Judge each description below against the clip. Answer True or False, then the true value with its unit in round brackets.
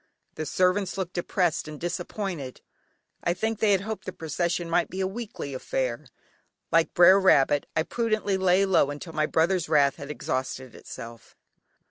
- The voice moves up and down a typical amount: True (4.5 semitones)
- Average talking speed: True (160 wpm)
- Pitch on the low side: False (175 Hz)